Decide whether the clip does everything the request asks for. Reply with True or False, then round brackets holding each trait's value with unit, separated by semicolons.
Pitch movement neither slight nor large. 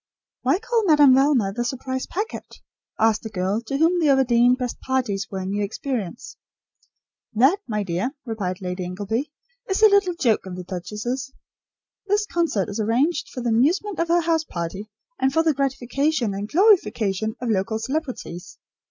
False (7.0 semitones)